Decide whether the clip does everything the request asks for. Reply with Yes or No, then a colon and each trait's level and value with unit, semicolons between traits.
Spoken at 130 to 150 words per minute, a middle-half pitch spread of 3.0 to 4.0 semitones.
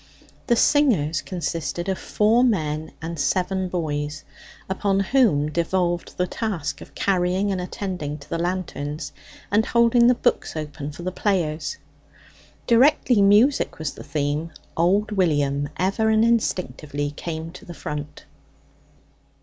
No: slow, 135 wpm; average, 5.2 semitones